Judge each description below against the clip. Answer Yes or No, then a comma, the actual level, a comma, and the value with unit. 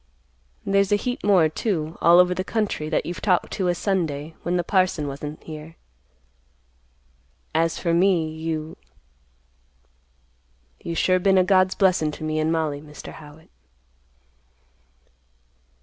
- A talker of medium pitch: Yes, medium, 160 Hz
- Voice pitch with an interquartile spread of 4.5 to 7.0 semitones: No, average, 4.1 semitones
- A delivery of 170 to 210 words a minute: No, slow, 135 wpm